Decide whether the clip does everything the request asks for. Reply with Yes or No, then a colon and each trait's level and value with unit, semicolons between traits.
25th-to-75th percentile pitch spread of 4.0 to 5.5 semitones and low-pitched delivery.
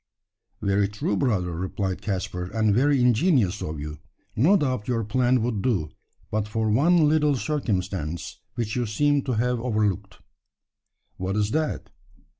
Yes: average, 4.7 semitones; low, 110 Hz